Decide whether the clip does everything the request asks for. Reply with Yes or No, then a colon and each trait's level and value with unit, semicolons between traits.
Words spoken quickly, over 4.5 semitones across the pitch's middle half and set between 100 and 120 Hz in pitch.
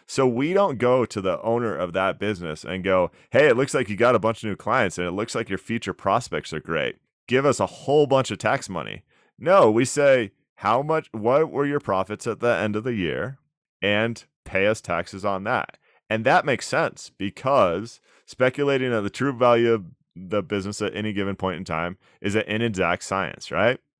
Yes: fast, 215 wpm; average, 4.9 semitones; low, 105 Hz